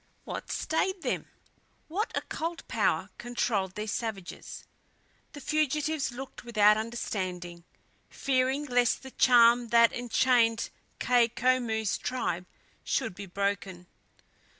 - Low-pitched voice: No, high, 235 Hz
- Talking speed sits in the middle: No, slow, 105 wpm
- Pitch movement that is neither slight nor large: Yes, average, 4.2 semitones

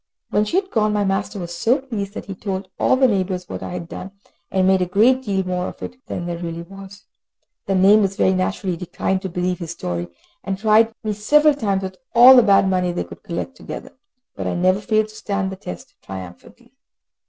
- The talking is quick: Yes, fast, 220 wpm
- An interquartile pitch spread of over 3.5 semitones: No, average, 2.9 semitones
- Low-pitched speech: No, high, 195 Hz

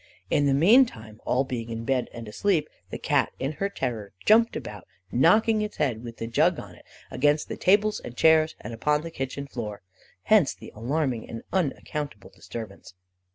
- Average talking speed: Yes, average, 180 wpm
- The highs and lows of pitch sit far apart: Yes, wide, 6.2 semitones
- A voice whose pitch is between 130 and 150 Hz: Yes, low, 135 Hz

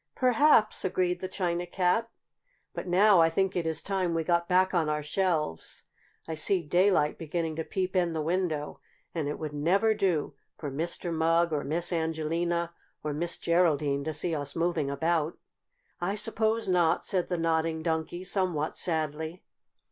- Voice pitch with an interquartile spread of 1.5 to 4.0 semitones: Yes, narrow, 2.6 semitones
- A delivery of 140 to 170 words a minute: Yes, average, 165 wpm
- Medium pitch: Yes, medium, 170 Hz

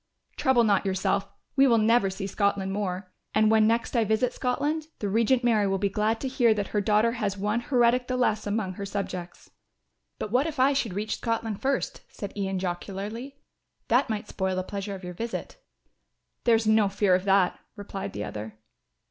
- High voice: Yes, high, 215 Hz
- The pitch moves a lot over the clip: No, average, 3.3 semitones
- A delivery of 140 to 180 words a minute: No, average, 195 wpm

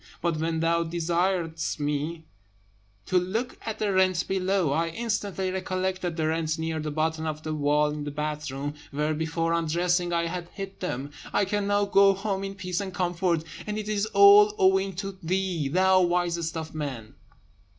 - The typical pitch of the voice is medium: Yes, medium, 175 Hz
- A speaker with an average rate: Yes, average, 175 wpm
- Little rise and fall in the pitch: No, average, 3.3 semitones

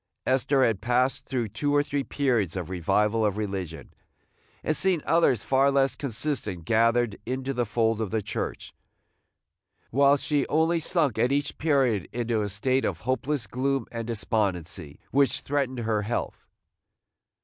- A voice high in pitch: No, low, 120 Hz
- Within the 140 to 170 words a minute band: Yes, average, 150 wpm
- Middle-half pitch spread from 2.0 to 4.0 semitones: No, average, 4.5 semitones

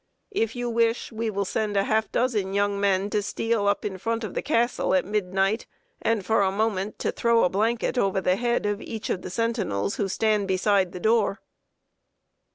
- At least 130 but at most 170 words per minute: No, average, 200 wpm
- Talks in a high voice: Yes, high, 210 Hz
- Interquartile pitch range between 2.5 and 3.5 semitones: Yes, average, 2.8 semitones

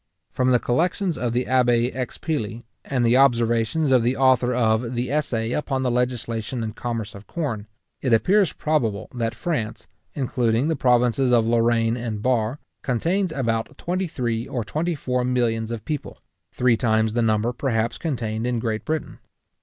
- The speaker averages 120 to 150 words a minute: No, average, 165 wpm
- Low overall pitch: Yes, low, 120 Hz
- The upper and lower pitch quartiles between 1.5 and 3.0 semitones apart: Yes, average, 2.7 semitones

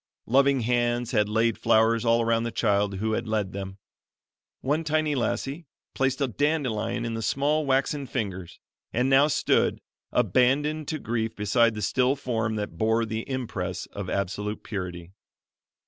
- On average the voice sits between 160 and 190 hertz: No, low, 115 Hz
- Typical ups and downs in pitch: Yes, average, 4.0 semitones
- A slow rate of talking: No, average, 155 wpm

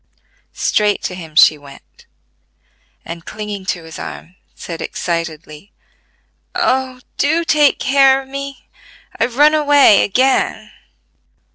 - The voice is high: Yes, high, 225 Hz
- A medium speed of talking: No, slow, 115 wpm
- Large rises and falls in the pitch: Yes, wide, 8.7 semitones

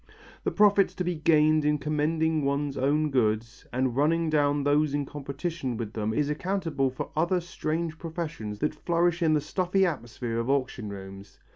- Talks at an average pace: Yes, average, 170 wpm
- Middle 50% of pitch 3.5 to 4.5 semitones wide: Yes, average, 4.1 semitones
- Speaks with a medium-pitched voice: Yes, medium, 150 Hz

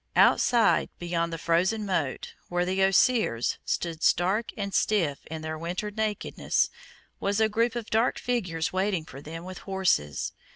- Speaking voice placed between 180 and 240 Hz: Yes, medium, 185 Hz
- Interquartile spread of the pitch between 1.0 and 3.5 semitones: No, average, 4.3 semitones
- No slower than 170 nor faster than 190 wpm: No, average, 155 wpm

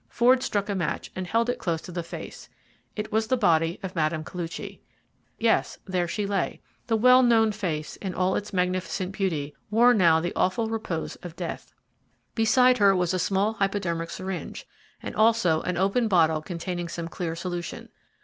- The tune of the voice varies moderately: Yes, average, 4.2 semitones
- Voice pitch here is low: No, medium, 185 Hz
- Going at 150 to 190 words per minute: Yes, average, 180 wpm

